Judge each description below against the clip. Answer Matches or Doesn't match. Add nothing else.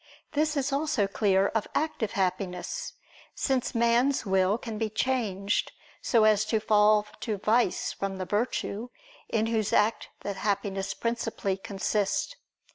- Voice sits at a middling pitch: Doesn't match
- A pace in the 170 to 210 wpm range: Doesn't match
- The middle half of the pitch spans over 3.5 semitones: Doesn't match